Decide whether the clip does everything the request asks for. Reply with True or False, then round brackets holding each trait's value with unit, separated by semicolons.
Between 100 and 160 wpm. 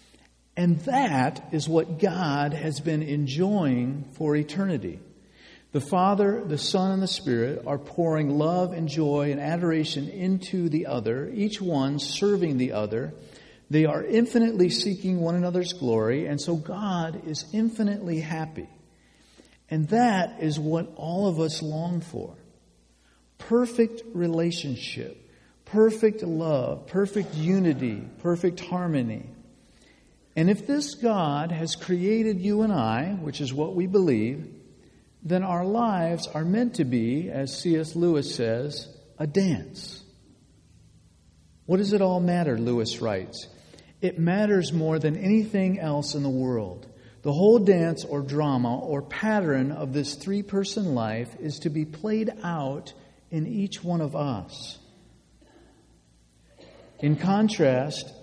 True (135 wpm)